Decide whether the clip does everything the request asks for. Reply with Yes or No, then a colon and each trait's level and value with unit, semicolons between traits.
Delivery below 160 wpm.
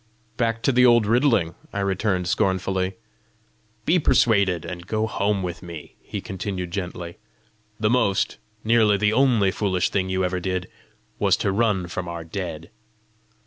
Yes: average, 150 wpm